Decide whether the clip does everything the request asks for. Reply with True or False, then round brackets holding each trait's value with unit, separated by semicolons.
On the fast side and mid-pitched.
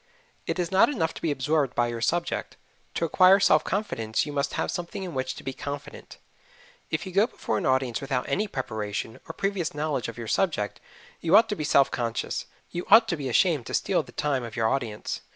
True (220 wpm; 145 Hz)